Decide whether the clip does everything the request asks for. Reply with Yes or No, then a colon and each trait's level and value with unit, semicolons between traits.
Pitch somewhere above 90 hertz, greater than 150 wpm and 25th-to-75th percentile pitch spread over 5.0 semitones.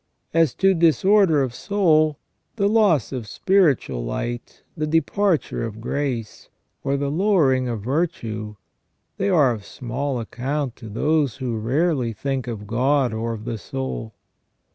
No: low, 135 Hz; average, 140 wpm; wide, 5.6 semitones